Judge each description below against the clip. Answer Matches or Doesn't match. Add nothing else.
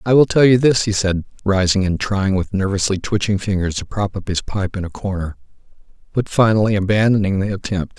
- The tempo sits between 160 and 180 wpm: Doesn't match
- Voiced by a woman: Doesn't match